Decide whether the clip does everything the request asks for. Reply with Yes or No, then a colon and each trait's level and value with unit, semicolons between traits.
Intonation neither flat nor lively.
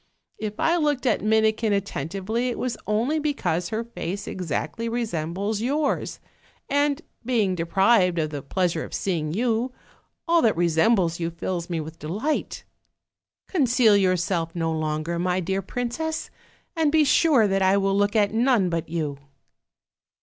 No: wide, 5.8 semitones